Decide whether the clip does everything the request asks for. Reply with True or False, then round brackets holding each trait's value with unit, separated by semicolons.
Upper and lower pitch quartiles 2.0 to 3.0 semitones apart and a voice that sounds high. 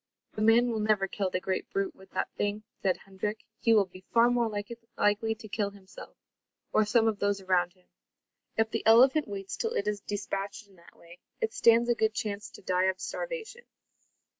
True (2.7 semitones; 210 Hz)